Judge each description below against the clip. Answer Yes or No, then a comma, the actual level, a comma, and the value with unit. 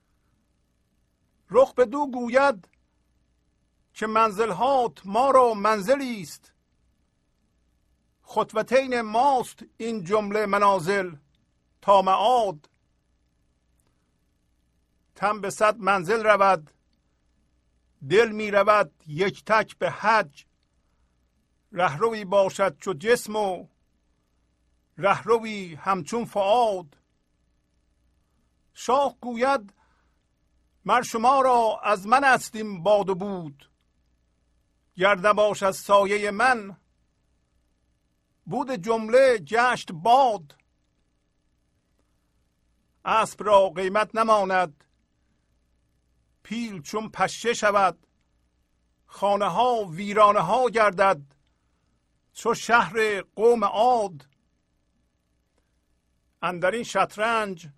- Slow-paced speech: Yes, slow, 80 wpm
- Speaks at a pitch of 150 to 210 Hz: Yes, medium, 185 Hz